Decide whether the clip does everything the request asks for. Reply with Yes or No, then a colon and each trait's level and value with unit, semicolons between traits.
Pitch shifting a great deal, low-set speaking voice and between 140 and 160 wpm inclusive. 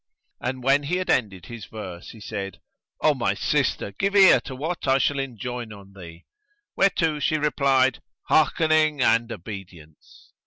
Yes: wide, 6.8 semitones; low, 125 Hz; average, 155 wpm